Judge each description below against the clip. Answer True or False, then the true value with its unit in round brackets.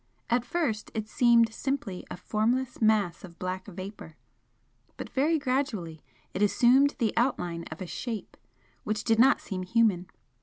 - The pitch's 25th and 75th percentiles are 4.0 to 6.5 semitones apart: True (5.0 semitones)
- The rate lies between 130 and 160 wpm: True (150 wpm)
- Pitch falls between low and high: False (220 Hz)